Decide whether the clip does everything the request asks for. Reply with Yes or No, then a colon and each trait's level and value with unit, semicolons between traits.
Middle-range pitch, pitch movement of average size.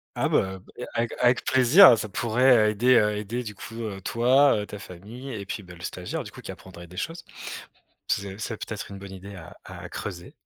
No: low, 105 Hz; average, 4.1 semitones